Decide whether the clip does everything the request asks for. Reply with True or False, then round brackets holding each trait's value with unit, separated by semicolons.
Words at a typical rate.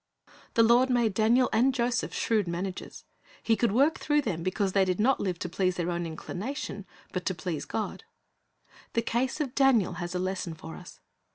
True (190 wpm)